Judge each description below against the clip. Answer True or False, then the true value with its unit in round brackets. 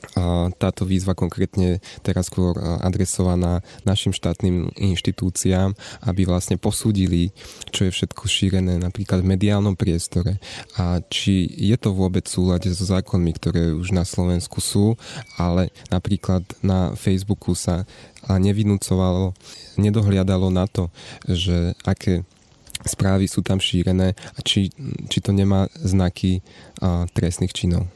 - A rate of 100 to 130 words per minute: True (120 wpm)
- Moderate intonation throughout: False (2.0 semitones)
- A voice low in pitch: True (95 Hz)